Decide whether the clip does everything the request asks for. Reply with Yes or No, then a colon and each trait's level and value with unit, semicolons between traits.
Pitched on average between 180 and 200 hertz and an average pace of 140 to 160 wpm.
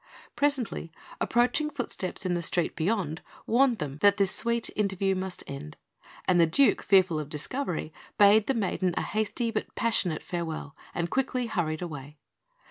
Yes: high, 190 Hz; average, 155 wpm